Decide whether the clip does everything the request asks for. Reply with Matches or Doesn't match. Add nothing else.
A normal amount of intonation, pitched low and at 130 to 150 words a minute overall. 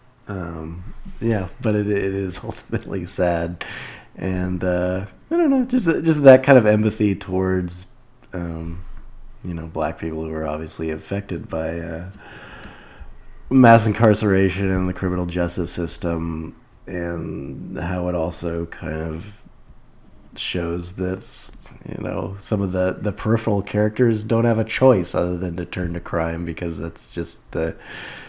Matches